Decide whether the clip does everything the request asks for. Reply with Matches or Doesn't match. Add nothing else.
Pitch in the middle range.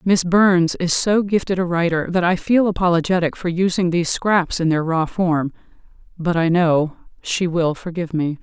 Matches